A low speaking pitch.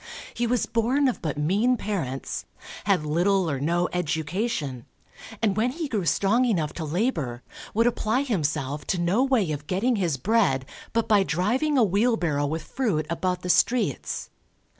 No: high, 190 Hz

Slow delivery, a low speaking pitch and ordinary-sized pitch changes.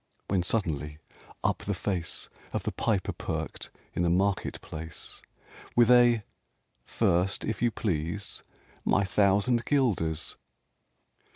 Yes: slow, 115 wpm; low, 100 Hz; average, 4.7 semitones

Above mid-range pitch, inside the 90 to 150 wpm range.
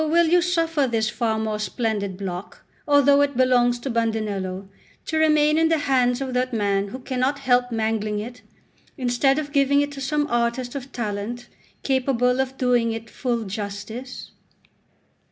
No: high, 245 Hz; average, 160 wpm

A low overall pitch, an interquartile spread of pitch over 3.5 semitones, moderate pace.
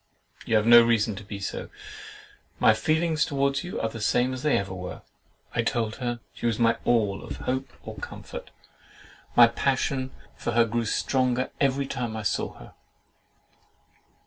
No: low, 120 Hz; average, 3.1 semitones; average, 170 wpm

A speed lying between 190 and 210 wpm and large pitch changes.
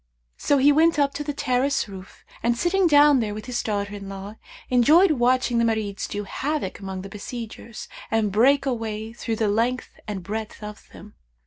No: average, 195 wpm; average, 4.9 semitones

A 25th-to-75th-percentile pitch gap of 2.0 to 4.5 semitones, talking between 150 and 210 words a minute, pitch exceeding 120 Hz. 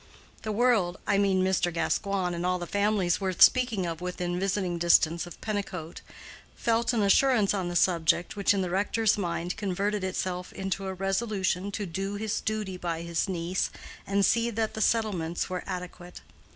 Yes: narrow, 2.6 semitones; average, 165 wpm; high, 190 Hz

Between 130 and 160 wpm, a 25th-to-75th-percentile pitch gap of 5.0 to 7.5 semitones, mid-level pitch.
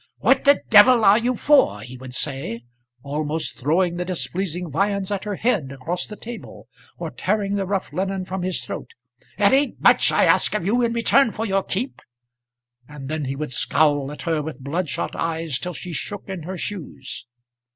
No: average, 195 wpm; wide, 5.4 semitones; medium, 180 Hz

